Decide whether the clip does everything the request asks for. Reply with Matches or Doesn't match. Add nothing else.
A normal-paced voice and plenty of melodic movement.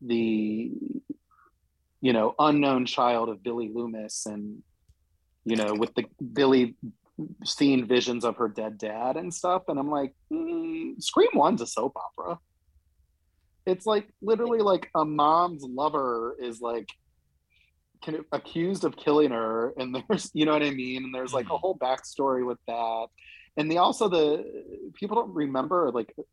Matches